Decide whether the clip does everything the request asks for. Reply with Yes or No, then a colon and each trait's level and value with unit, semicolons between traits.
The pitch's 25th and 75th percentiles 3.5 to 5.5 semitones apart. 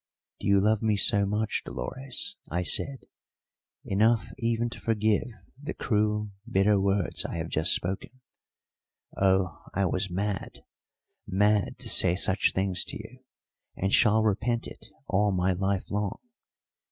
No: narrow, 2.4 semitones